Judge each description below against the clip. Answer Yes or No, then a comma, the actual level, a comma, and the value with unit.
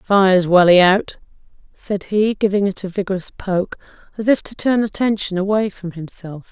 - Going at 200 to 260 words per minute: No, average, 165 wpm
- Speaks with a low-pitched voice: No, high, 195 Hz